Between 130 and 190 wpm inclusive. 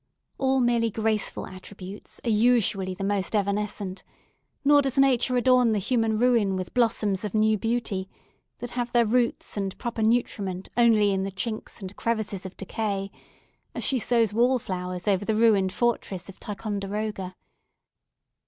Yes: average, 155 wpm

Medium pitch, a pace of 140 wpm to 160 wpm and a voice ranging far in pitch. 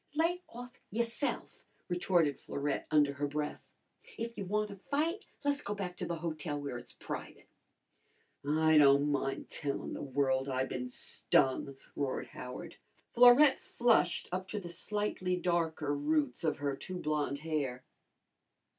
Yes: medium, 160 Hz; average, 145 wpm; wide, 6.4 semitones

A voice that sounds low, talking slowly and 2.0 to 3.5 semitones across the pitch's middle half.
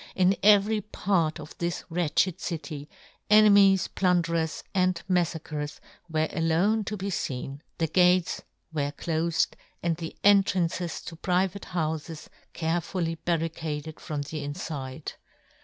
No: medium, 170 Hz; slow, 125 wpm; average, 2.8 semitones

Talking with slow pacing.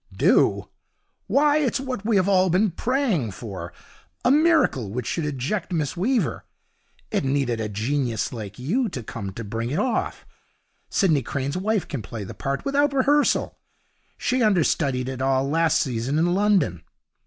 No: average, 160 wpm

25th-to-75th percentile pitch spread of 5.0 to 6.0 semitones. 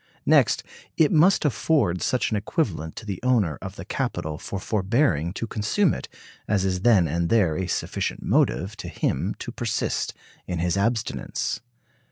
Yes: average, 5.3 semitones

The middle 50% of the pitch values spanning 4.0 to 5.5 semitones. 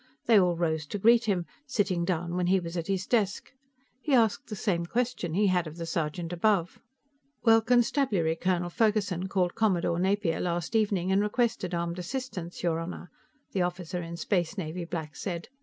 No: average, 3.6 semitones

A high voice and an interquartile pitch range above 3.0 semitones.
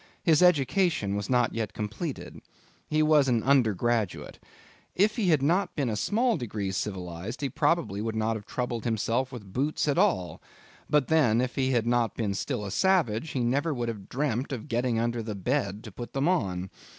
No: low, 120 Hz; wide, 5.4 semitones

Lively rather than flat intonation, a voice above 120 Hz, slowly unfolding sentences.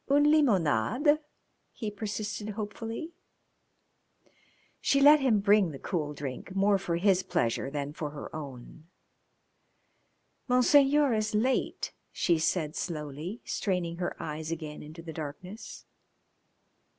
Yes: wide, 6.6 semitones; high, 190 Hz; slow, 115 wpm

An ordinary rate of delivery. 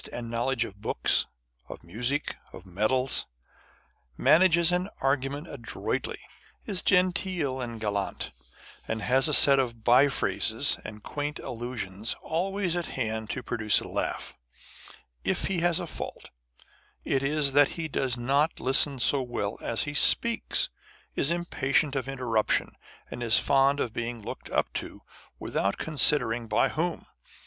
Yes: average, 150 wpm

